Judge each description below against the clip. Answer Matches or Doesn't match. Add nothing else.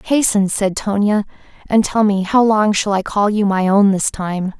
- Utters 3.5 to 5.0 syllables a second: Matches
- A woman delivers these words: Matches